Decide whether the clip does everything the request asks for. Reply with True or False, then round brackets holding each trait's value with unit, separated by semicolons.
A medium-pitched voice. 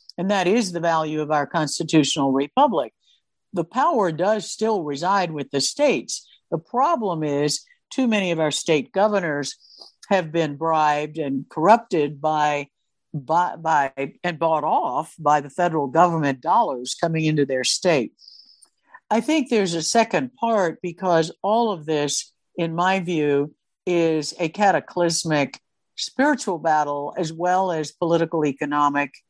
True (165 Hz)